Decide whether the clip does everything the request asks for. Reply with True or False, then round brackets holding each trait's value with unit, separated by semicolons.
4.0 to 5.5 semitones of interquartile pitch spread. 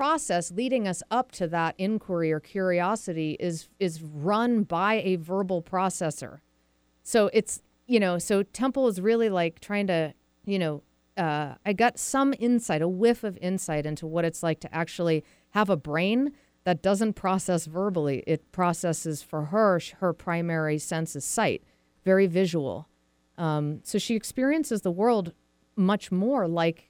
True (4.6 semitones)